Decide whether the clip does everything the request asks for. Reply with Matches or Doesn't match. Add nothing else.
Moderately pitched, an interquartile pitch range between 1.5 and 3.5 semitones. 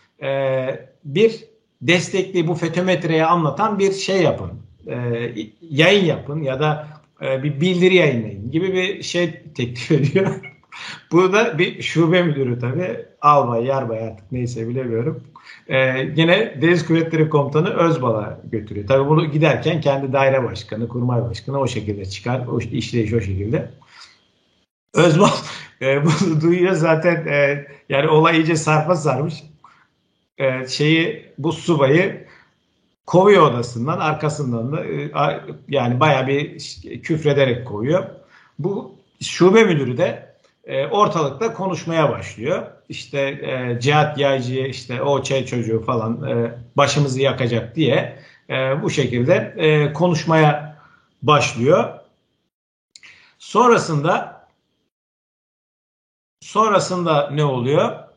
Doesn't match